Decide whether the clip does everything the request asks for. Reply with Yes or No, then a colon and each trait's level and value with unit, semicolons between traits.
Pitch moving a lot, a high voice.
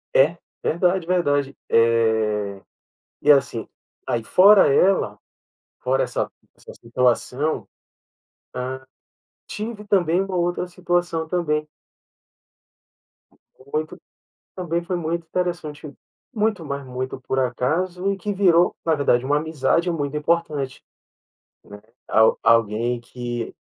No: wide, 5.8 semitones; medium, 150 Hz